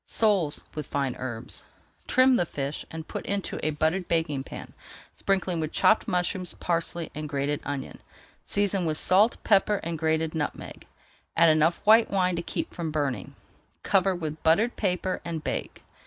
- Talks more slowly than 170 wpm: Yes, average, 160 wpm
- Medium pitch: Yes, medium, 165 Hz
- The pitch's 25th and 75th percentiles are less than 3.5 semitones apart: No, average, 3.8 semitones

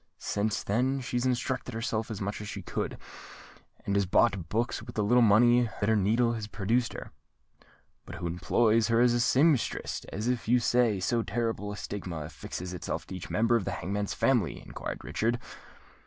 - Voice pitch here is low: Yes, low, 115 Hz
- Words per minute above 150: Yes, average, 185 wpm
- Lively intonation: No, average, 3.0 semitones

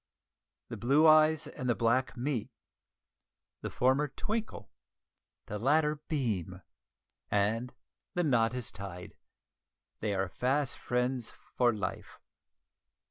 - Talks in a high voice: No, low, 125 Hz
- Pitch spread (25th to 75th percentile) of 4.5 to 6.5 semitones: Yes, average, 5.2 semitones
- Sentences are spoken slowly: Yes, slow, 110 wpm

